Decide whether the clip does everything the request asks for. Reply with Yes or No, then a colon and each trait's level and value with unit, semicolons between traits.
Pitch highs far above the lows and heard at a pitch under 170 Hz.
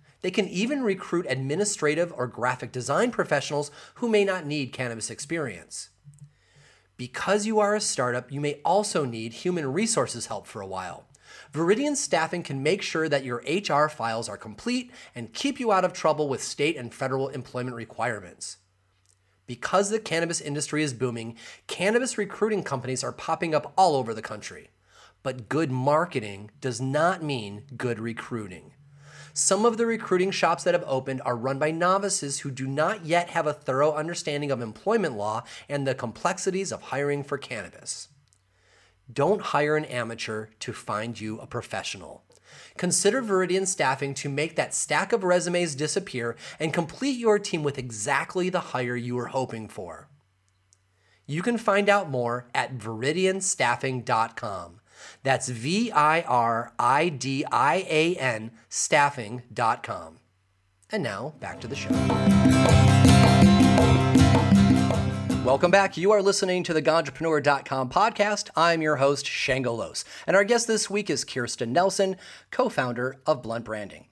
Yes: wide, 6.5 semitones; medium, 140 Hz